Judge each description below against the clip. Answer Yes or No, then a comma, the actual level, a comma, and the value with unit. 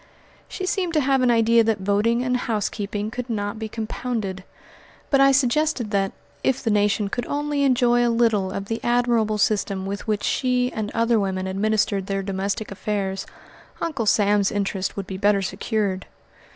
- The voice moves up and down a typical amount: Yes, average, 3.4 semitones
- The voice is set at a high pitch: Yes, high, 215 Hz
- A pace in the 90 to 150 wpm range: No, average, 170 wpm